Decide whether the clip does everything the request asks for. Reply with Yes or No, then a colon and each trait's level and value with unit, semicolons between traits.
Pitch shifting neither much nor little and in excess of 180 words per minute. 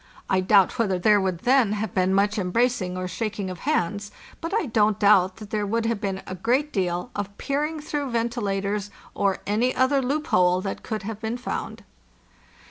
Yes: average, 4.0 semitones; average, 195 wpm